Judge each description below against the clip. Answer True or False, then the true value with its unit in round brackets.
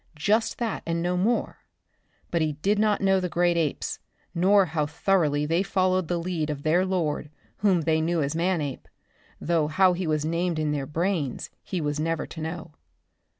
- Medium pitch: True (170 Hz)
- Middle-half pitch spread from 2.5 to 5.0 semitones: True (3.2 semitones)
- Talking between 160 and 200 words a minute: True (185 wpm)